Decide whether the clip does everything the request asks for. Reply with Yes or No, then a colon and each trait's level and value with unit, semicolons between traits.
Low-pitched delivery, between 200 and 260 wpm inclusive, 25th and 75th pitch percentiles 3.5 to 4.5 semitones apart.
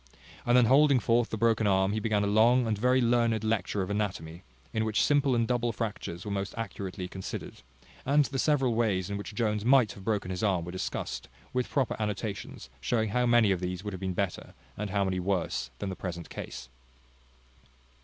Yes: low, 105 Hz; fast, 205 wpm; average, 3.8 semitones